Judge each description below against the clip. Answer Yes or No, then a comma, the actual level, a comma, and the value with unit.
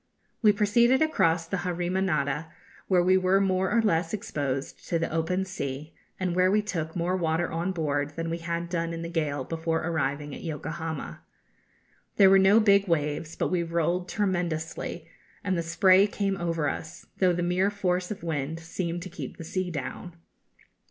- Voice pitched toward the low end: No, medium, 170 Hz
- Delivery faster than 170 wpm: Yes, average, 185 wpm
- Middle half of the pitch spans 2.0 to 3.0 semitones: Yes, narrow, 2.5 semitones